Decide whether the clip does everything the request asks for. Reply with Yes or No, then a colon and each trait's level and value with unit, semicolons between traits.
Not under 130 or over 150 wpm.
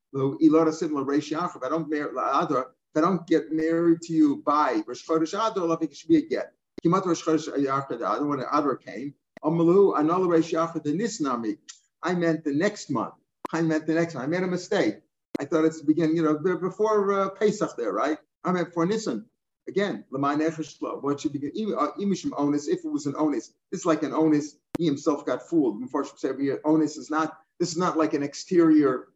No: average, 180 wpm